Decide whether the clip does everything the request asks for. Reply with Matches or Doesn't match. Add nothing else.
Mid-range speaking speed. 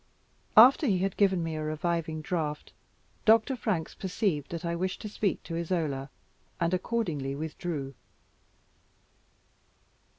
Doesn't match